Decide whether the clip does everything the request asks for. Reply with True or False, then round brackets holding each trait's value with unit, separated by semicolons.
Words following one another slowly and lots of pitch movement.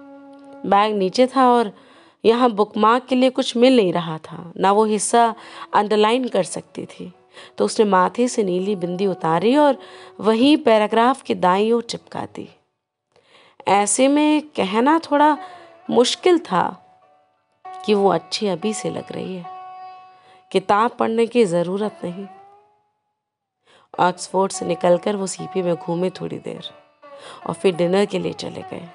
False (145 wpm; 6.6 semitones)